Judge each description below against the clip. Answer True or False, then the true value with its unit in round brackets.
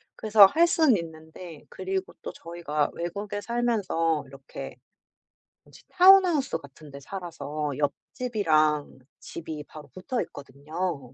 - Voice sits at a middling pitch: True (170 Hz)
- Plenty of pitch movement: True (5.7 semitones)